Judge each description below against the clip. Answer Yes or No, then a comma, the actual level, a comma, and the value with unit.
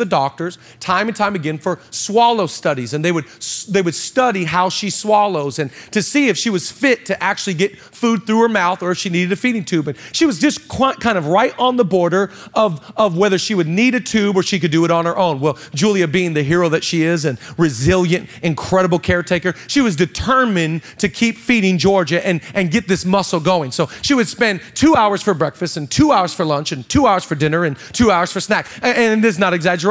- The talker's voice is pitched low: No, medium, 185 Hz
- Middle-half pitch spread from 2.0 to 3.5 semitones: No, average, 4.2 semitones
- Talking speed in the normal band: No, fast, 240 wpm